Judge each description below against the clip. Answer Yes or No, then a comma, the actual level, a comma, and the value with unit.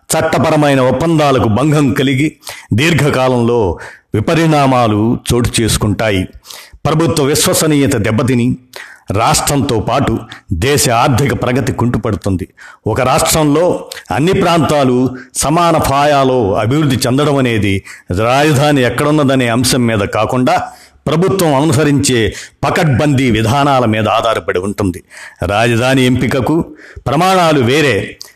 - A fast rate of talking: No, average, 90 wpm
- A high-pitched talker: No, low, 130 Hz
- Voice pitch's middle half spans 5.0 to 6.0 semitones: No, average, 4.2 semitones